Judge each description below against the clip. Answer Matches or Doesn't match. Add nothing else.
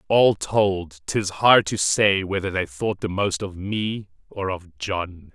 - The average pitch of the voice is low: Matches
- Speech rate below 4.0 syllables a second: Matches